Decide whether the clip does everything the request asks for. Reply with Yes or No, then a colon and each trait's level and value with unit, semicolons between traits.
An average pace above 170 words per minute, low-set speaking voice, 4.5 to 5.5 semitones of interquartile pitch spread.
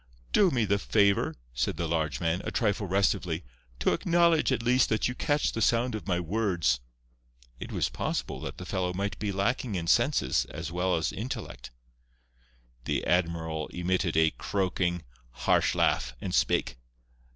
No: average, 160 wpm; very low, 95 Hz; average, 5.1 semitones